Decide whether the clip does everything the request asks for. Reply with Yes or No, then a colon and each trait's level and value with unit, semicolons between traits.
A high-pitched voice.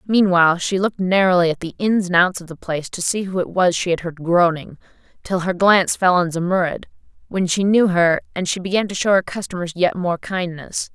No: medium, 180 Hz